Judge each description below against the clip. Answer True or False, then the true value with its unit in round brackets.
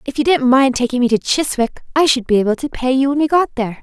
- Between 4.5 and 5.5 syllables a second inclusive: False (6.4 syllables/s)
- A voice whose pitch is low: False (260 Hz)